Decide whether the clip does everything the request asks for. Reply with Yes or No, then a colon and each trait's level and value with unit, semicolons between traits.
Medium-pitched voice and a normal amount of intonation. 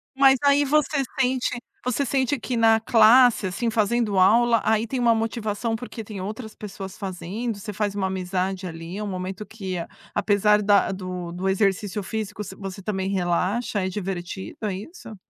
No: high, 210 Hz; average, 3.4 semitones